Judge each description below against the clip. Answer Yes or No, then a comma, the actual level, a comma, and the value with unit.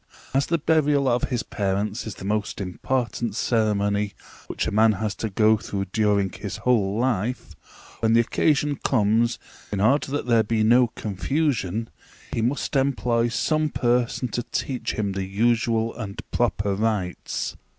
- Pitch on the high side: No, low, 115 Hz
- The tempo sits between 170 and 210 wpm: No, average, 155 wpm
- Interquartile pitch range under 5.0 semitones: Yes, average, 3.3 semitones